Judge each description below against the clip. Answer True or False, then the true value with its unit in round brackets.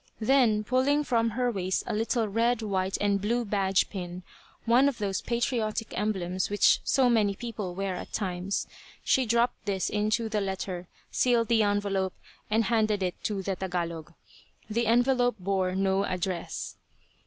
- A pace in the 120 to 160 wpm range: True (155 wpm)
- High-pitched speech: True (210 Hz)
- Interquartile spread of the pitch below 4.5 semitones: True (3.5 semitones)